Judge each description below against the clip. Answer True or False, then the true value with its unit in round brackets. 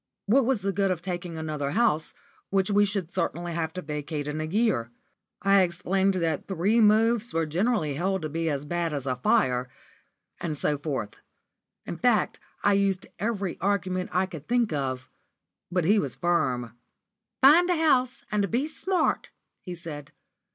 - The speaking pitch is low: False (180 Hz)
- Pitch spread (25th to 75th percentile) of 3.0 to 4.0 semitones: False (4.8 semitones)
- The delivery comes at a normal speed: True (170 wpm)